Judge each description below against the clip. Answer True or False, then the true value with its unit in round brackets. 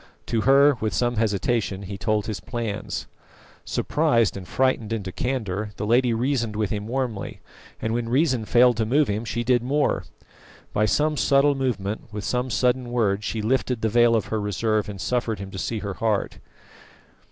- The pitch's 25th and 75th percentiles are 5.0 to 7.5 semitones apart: False (3.1 semitones)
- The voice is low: True (115 Hz)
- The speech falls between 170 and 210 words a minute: True (180 wpm)